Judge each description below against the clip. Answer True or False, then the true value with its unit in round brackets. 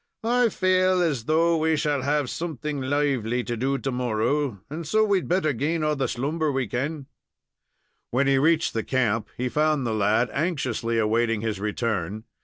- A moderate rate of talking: True (175 wpm)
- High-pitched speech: False (135 Hz)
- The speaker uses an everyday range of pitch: True (5.0 semitones)